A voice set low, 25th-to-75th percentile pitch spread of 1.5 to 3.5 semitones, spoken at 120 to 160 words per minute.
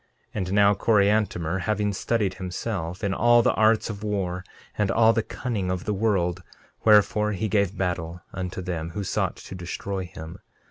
No: low, 100 Hz; average, 2.7 semitones; average, 175 wpm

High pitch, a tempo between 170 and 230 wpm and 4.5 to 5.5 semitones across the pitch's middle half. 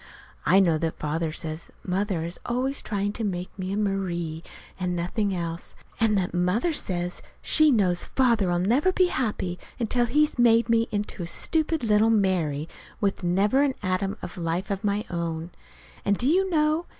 Yes: high, 195 Hz; average, 175 wpm; average, 5.0 semitones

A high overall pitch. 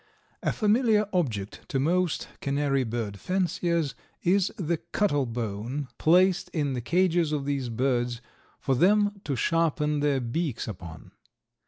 No: medium, 145 Hz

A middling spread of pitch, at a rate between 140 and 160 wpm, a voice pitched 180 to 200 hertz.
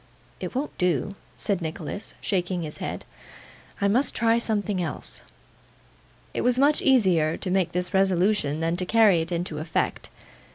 Yes: average, 4.4 semitones; average, 155 wpm; medium, 185 Hz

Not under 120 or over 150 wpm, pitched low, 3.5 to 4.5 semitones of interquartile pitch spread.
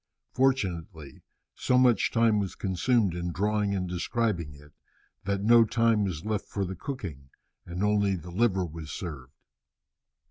Yes: average, 145 wpm; very low, 95 Hz; average, 4.2 semitones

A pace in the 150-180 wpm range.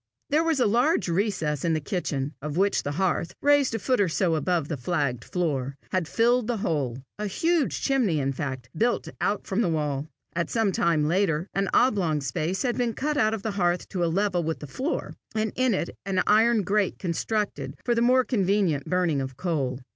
No: fast, 205 wpm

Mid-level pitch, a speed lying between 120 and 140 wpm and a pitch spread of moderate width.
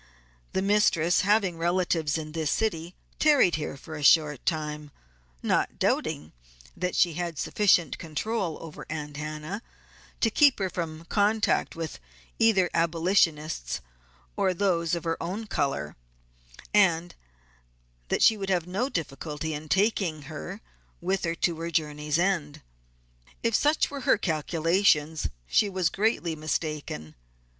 Yes: medium, 170 Hz; slow, 135 wpm; average, 4.0 semitones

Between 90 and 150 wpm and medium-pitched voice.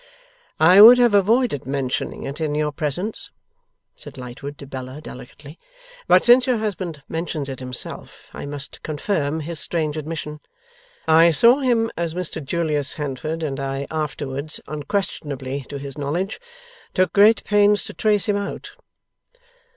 Yes: average, 145 wpm; medium, 155 Hz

